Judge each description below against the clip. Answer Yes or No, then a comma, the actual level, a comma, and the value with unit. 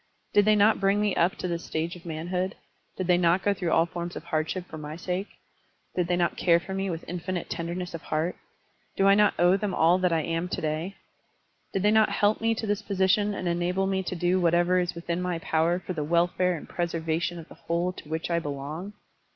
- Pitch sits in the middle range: Yes, medium, 175 Hz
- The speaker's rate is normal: No, fast, 235 wpm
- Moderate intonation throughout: No, narrow, 2.2 semitones